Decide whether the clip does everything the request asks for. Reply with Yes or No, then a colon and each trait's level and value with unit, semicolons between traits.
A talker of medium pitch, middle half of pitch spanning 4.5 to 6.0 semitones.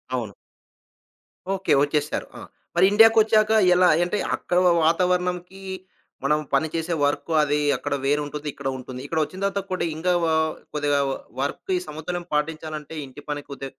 No: medium, 160 Hz; average, 3.8 semitones